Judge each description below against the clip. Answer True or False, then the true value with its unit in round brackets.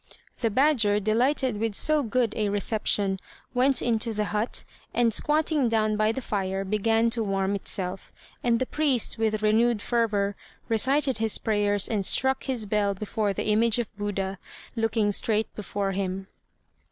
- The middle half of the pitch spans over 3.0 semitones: False (2.6 semitones)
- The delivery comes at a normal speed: True (155 wpm)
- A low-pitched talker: False (215 Hz)